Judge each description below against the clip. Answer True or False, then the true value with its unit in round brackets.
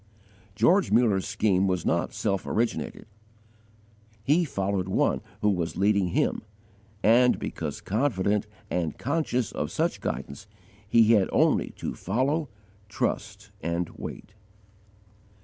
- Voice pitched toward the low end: True (105 Hz)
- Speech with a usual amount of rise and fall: True (4.2 semitones)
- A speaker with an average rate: False (115 wpm)